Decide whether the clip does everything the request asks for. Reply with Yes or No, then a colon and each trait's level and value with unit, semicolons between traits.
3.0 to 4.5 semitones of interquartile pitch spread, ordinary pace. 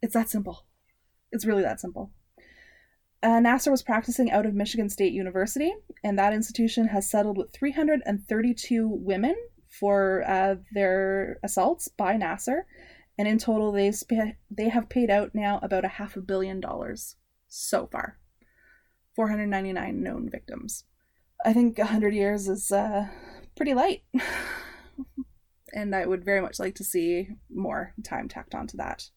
Yes: average, 3.5 semitones; average, 150 wpm